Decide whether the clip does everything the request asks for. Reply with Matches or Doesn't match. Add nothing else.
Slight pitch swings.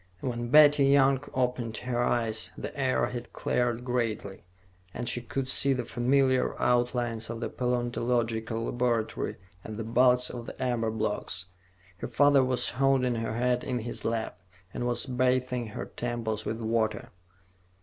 Matches